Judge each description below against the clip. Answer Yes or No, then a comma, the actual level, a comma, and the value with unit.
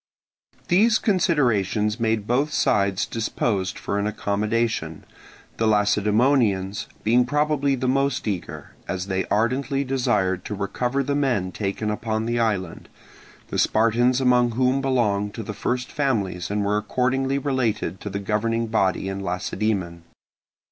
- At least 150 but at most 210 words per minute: No, slow, 135 wpm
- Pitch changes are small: No, average, 4.2 semitones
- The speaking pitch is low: Yes, low, 110 Hz